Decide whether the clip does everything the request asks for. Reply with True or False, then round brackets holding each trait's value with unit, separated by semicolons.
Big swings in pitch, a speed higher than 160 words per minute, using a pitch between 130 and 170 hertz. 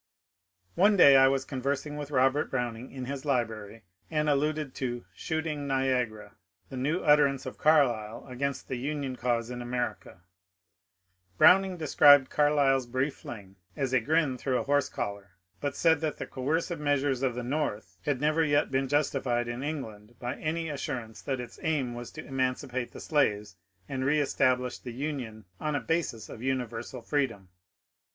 False (3.3 semitones; 170 wpm; 135 Hz)